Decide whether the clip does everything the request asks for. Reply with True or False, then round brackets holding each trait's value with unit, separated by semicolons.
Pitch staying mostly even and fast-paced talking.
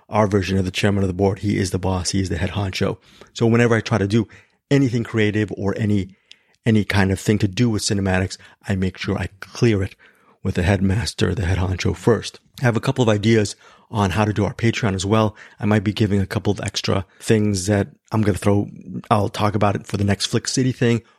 True (2.2 semitones; 240 wpm)